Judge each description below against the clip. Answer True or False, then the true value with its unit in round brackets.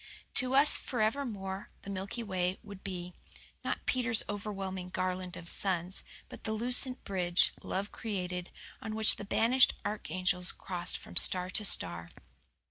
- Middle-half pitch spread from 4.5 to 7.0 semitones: False (3.2 semitones)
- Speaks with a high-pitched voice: True (195 Hz)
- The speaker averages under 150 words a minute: True (140 wpm)